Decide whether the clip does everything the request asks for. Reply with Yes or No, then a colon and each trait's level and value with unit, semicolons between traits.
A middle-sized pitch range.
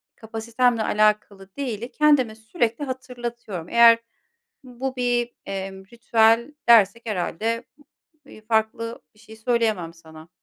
No: narrow, 2.2 semitones